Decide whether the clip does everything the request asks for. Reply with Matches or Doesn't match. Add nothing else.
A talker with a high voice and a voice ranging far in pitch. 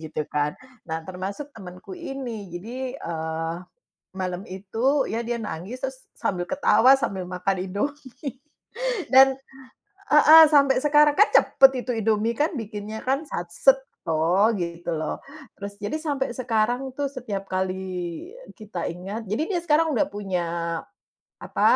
Matches